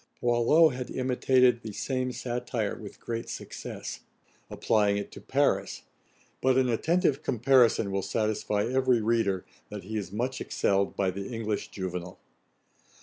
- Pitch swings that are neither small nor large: Yes, average, 3.8 semitones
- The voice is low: Yes, low, 115 Hz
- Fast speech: No, average, 140 wpm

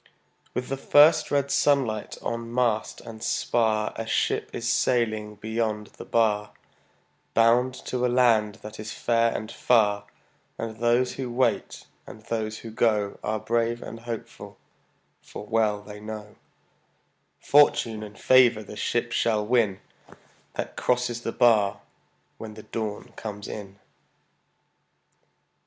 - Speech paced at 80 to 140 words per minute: Yes, slow, 135 wpm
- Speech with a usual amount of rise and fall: No, narrow, 1.9 semitones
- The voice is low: Yes, low, 115 Hz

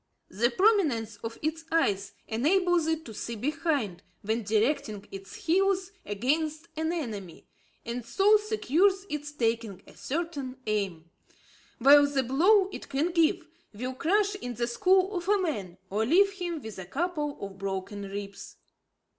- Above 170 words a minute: No, average, 150 wpm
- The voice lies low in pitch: No, very high, 285 Hz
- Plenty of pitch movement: Yes, wide, 8.0 semitones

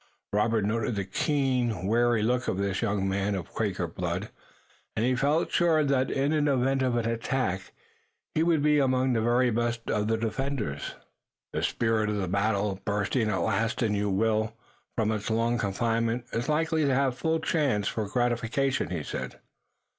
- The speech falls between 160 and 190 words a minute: Yes, average, 175 wpm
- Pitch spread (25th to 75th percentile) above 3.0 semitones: Yes, average, 4.1 semitones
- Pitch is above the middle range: No, low, 115 Hz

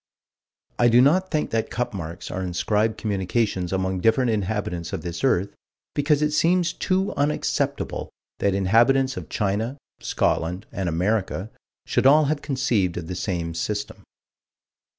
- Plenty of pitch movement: Yes, wide, 6.3 semitones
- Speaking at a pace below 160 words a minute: Yes, average, 145 wpm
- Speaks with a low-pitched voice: Yes, low, 105 Hz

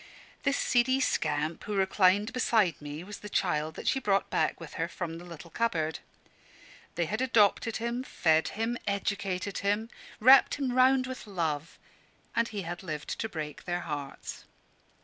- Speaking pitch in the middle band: No, high, 195 Hz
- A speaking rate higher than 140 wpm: Yes, average, 165 wpm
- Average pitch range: No, wide, 5.9 semitones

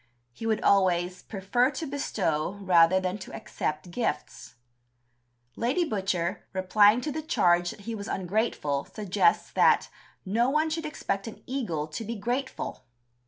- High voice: Yes, high, 200 Hz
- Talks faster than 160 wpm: No, average, 145 wpm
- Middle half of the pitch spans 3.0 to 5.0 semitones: No, wide, 5.4 semitones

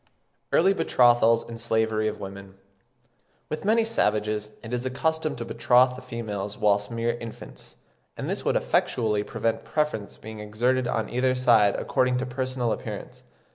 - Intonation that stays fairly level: No, average, 3.0 semitones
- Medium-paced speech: Yes, average, 155 wpm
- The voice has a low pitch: Yes, low, 115 Hz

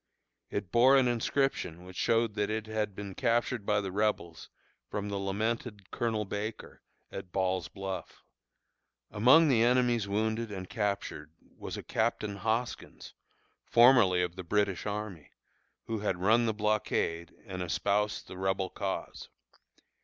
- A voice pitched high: No, low, 105 Hz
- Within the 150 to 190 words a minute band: No, average, 140 wpm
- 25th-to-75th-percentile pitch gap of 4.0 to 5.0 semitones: No, average, 3.0 semitones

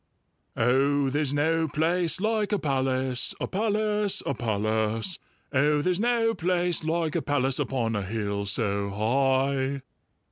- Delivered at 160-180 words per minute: No, slow, 135 wpm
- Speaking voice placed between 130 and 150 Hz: Yes, medium, 140 Hz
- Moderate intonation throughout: No, wide, 6.0 semitones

